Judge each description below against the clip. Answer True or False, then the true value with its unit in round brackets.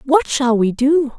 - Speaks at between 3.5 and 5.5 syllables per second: True (3.9 syllables/s)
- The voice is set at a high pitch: True (265 Hz)